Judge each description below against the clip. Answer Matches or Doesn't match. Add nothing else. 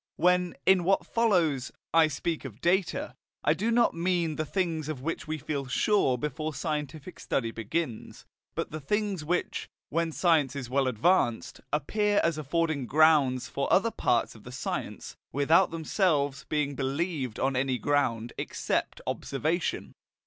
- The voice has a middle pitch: Matches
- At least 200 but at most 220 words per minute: Doesn't match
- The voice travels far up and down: Doesn't match